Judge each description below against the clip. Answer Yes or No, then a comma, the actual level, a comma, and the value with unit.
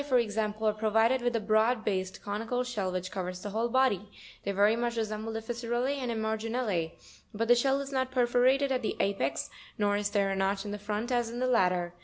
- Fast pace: Yes, fast, 225 wpm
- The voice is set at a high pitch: Yes, high, 220 Hz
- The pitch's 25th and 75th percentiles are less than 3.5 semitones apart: Yes, average, 3.1 semitones